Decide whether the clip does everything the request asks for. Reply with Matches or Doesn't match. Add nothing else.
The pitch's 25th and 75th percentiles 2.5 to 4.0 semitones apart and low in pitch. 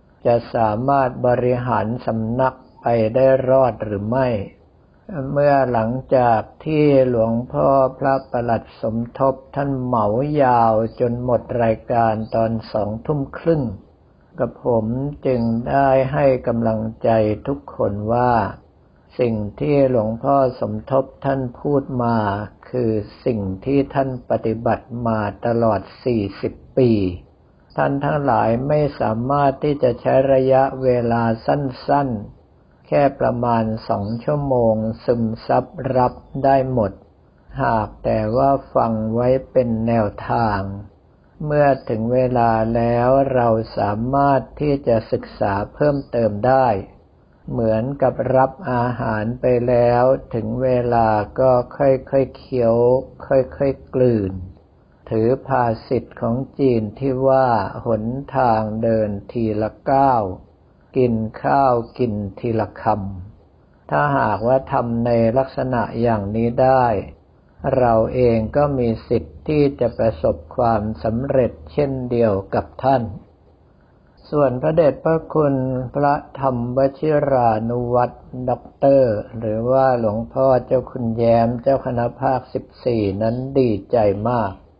Matches